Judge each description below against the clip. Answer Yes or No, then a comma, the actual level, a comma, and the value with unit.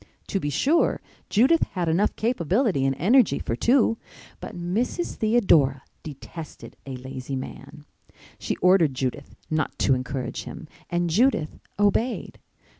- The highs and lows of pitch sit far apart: Yes, wide, 8.4 semitones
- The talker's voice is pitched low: No, medium, 175 Hz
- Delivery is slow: Yes, slow, 130 wpm